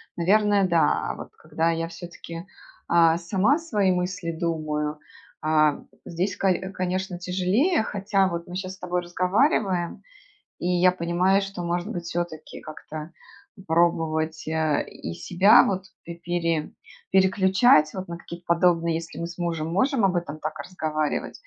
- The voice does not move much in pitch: Yes, narrow, 2.3 semitones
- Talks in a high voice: No, medium, 175 Hz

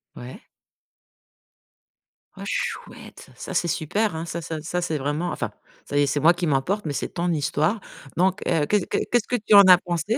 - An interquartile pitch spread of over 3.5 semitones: Yes, average, 4.7 semitones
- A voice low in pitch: No, medium, 170 Hz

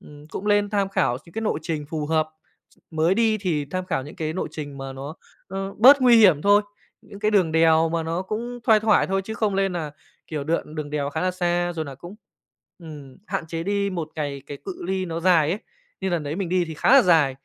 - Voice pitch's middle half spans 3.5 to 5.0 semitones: Yes, average, 4.3 semitones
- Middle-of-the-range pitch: Yes, medium, 170 Hz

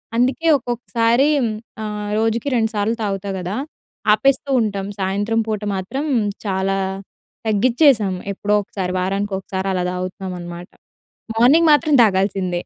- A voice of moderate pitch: No, high, 205 Hz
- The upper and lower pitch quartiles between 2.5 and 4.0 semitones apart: Yes, average, 3.5 semitones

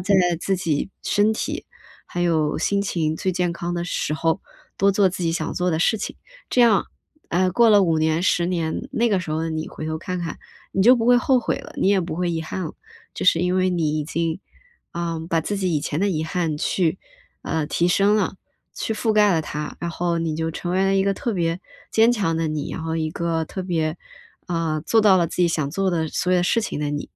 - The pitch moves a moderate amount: Yes, average, 3.2 semitones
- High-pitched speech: No, medium, 175 Hz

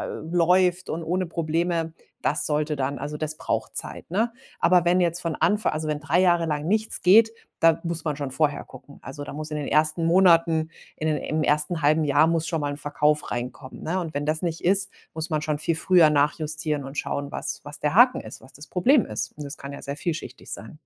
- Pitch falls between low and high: Yes, medium, 155 Hz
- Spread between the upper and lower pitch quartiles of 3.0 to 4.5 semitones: No, narrow, 2.6 semitones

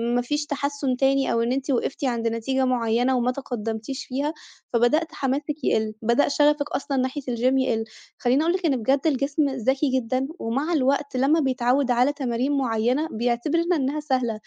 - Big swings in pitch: No, average, 2.9 semitones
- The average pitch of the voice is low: No, very high, 265 Hz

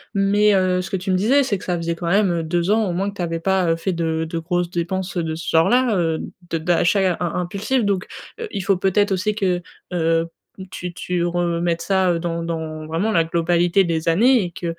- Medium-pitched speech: Yes, medium, 175 Hz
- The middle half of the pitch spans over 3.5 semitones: No, average, 2.7 semitones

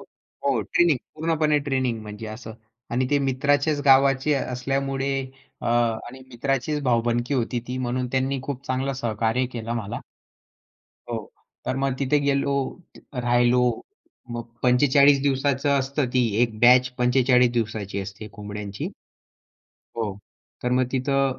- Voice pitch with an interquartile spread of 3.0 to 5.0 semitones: No, narrow, 2.5 semitones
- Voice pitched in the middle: No, low, 130 Hz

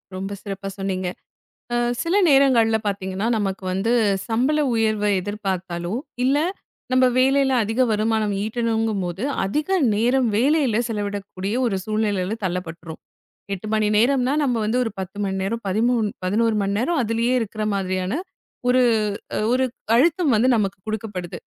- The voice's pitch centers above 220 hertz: No, high, 215 Hz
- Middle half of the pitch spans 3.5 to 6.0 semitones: Yes, average, 3.9 semitones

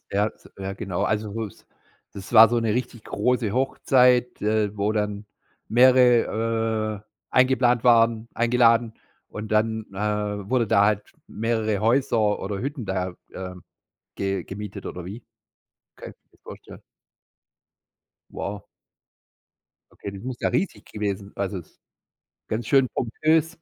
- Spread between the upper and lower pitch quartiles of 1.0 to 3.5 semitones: Yes, average, 2.9 semitones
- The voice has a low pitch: Yes, low, 110 Hz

